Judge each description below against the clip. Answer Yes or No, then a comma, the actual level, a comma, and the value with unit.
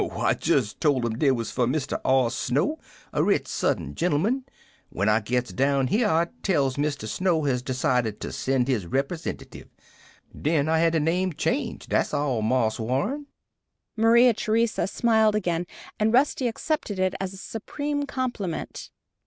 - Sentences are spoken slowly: No, average, 160 wpm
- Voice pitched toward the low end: No, medium, 160 Hz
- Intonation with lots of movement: Yes, wide, 8.7 semitones